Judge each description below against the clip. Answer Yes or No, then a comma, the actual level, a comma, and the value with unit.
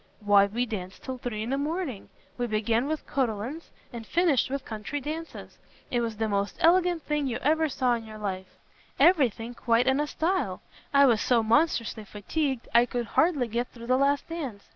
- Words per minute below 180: No, average, 195 wpm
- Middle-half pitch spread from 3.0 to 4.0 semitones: No, average, 5.0 semitones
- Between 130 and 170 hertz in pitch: No, high, 245 Hz